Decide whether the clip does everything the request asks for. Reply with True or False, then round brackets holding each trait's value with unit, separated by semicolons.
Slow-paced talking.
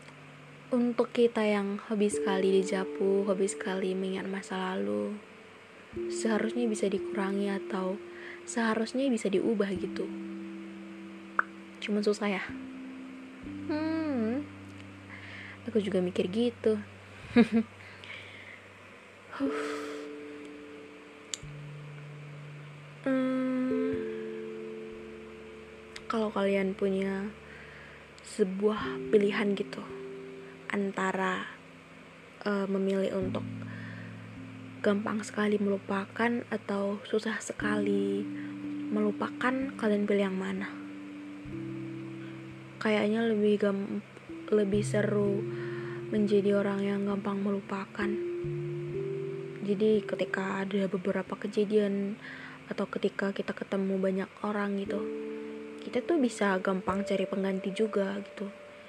True (80 wpm)